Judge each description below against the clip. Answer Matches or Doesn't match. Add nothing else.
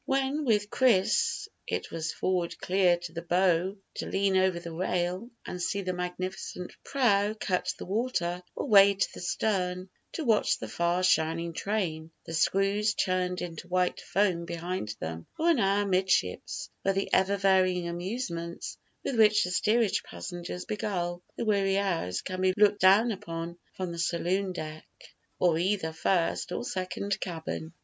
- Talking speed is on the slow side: Doesn't match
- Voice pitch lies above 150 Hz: Matches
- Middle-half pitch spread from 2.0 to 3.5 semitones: Matches